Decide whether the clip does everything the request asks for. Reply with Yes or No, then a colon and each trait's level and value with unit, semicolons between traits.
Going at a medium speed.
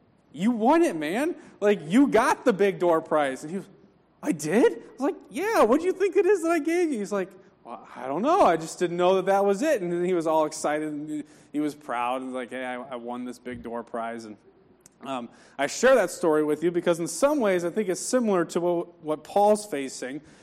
No: fast, 245 wpm